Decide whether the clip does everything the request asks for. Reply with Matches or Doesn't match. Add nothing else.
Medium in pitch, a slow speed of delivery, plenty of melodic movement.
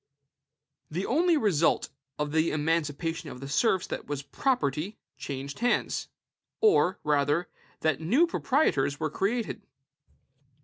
Matches